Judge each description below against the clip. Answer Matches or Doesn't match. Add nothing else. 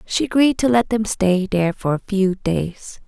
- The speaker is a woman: Matches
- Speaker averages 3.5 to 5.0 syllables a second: Matches